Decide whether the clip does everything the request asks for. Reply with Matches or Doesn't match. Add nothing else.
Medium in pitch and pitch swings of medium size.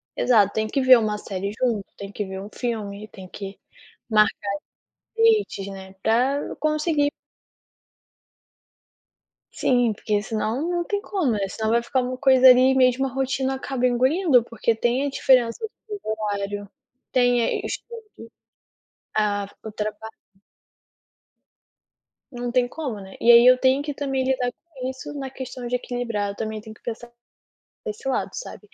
Doesn't match